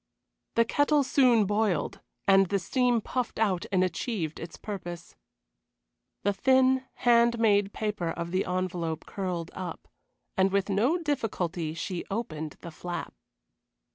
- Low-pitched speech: No, high, 195 Hz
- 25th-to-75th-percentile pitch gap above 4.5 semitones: Yes, average, 5.0 semitones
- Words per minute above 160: No, slow, 135 wpm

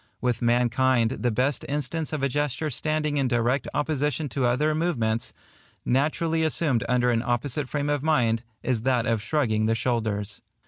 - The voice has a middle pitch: No, low, 130 Hz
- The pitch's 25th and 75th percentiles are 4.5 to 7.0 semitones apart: No, average, 3.9 semitones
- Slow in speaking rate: No, average, 165 wpm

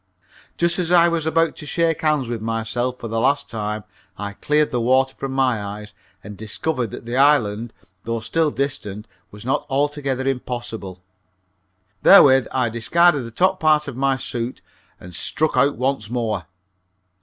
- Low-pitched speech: Yes, low, 130 Hz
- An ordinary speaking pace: Yes, average, 165 wpm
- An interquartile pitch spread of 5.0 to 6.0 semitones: No, average, 4.6 semitones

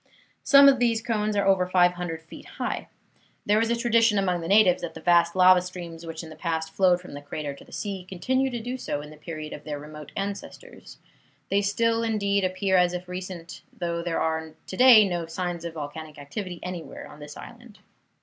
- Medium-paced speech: No, fast, 210 wpm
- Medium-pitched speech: Yes, medium, 180 Hz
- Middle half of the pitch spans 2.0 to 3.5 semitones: No, average, 4.1 semitones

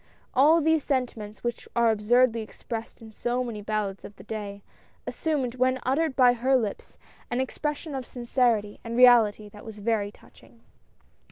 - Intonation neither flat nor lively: Yes, average, 3.2 semitones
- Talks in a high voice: Yes, high, 235 Hz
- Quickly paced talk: No, average, 160 wpm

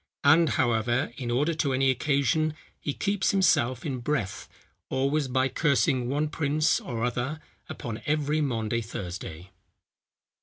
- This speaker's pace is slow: Yes, slow, 130 wpm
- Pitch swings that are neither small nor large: Yes, average, 4.1 semitones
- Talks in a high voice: No, low, 130 Hz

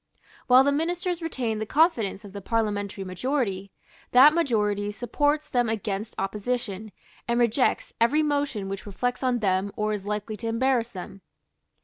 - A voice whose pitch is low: No, high, 225 Hz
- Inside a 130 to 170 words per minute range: Yes, average, 150 wpm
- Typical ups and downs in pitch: Yes, average, 4.4 semitones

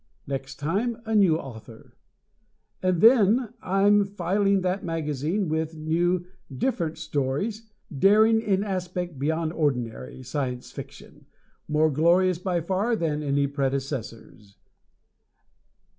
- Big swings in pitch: Yes, wide, 5.7 semitones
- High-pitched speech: No, medium, 165 Hz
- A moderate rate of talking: No, slow, 110 wpm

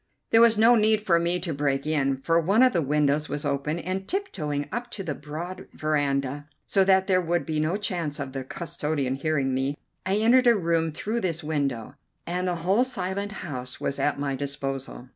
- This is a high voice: No, medium, 160 Hz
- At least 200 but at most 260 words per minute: Yes, fast, 205 wpm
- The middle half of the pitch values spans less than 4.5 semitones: No, average, 5.0 semitones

